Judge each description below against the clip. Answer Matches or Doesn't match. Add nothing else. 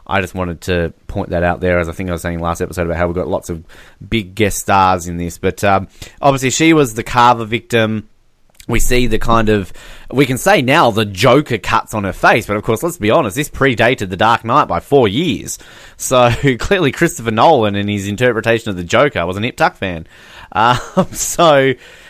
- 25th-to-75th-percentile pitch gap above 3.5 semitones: Matches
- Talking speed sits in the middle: Doesn't match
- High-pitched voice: Doesn't match